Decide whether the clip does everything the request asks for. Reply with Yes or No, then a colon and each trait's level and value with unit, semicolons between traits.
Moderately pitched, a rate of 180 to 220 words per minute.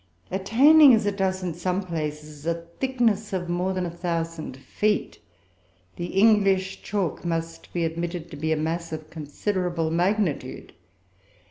No: medium, 175 Hz; average, 145 wpm